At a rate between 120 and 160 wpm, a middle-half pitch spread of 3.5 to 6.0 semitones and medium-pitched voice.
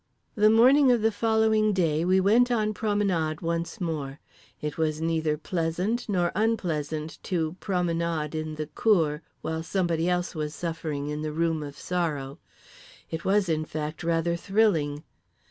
Yes: average, 150 wpm; average, 4.4 semitones; medium, 165 Hz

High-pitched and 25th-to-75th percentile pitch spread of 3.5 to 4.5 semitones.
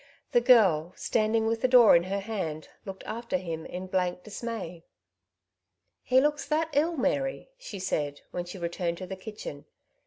No: high, 195 Hz; average, 5.2 semitones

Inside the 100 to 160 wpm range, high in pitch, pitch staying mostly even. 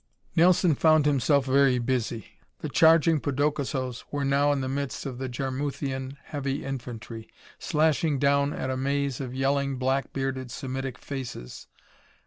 No: average, 140 wpm; low, 135 Hz; narrow, 1.6 semitones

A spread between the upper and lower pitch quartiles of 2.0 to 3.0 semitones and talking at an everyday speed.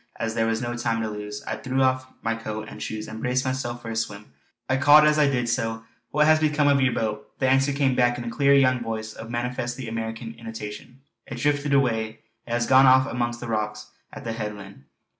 No: average, 2.7 semitones; fast, 230 wpm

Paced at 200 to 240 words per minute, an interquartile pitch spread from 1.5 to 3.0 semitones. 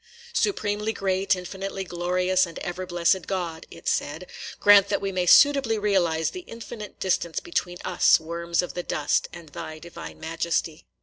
No: average, 160 wpm; average, 2.7 semitones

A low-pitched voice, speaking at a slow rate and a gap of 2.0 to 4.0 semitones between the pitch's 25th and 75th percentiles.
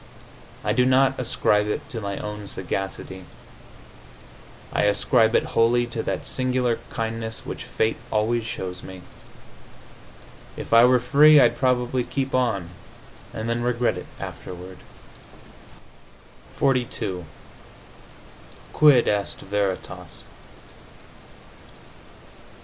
Yes: low, 115 Hz; slow, 105 wpm; average, 3.7 semitones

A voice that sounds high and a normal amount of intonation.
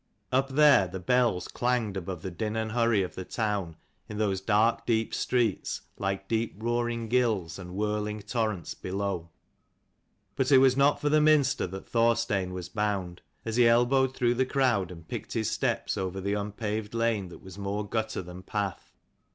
No: low, 105 Hz; average, 3.8 semitones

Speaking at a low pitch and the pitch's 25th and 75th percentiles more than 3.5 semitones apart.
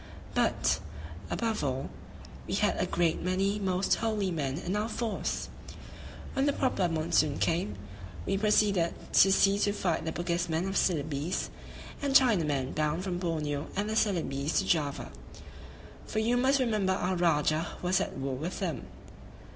No: medium, 180 Hz; average, 4.7 semitones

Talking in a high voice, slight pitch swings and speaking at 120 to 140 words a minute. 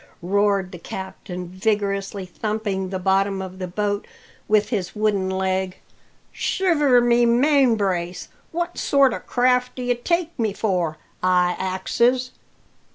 No: high, 200 Hz; average, 4.4 semitones; slow, 135 wpm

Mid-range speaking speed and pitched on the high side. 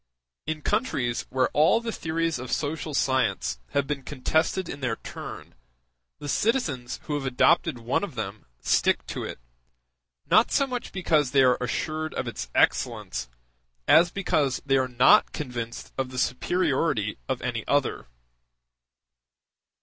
No: average, 145 wpm; medium, 140 Hz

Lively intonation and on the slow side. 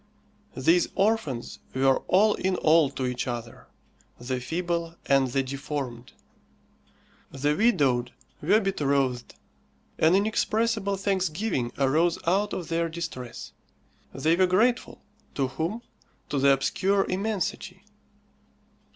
Yes: wide, 6.4 semitones; slow, 110 wpm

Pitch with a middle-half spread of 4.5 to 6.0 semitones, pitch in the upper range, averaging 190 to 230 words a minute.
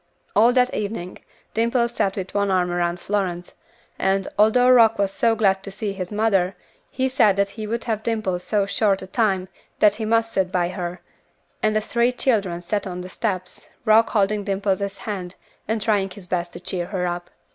No: average, 3.0 semitones; high, 200 Hz; average, 195 wpm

